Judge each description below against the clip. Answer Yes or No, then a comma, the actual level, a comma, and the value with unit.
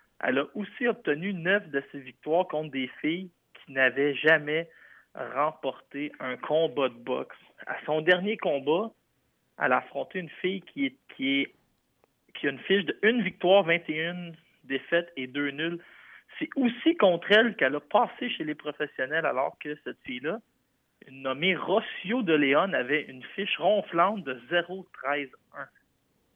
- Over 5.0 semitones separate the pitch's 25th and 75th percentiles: Yes, wide, 5.5 semitones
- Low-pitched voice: No, medium, 170 Hz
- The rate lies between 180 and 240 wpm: No, average, 155 wpm